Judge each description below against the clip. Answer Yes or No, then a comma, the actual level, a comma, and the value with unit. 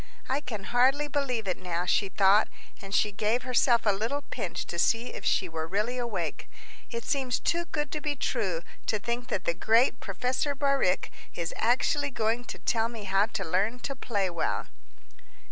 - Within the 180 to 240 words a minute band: Yes, average, 185 wpm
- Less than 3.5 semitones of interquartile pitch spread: No, average, 4.6 semitones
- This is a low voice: No, high, 230 Hz